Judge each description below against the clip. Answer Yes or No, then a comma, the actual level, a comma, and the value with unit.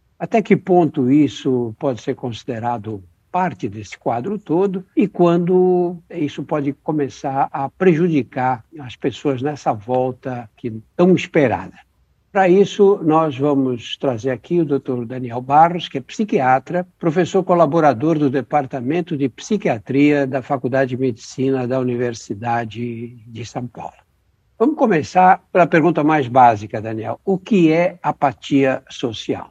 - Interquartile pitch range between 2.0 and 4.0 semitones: No, wide, 5.4 semitones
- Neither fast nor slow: Yes, average, 130 wpm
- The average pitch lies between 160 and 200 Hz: No, medium, 140 Hz